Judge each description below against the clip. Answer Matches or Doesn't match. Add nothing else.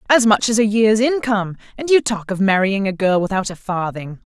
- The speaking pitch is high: Matches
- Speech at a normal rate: Doesn't match